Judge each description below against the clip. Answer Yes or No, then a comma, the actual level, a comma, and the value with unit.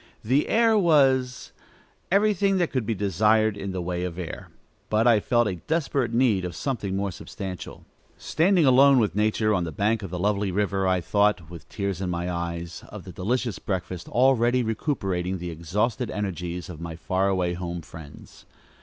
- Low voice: Yes, low, 100 Hz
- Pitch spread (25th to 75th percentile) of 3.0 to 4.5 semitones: No, wide, 5.4 semitones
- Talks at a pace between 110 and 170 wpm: No, average, 180 wpm